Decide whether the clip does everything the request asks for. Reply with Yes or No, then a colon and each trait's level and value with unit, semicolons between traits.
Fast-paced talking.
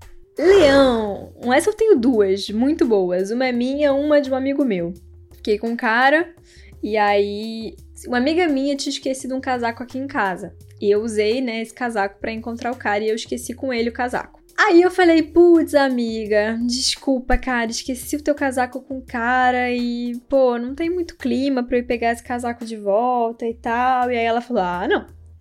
Yes: fast, 200 wpm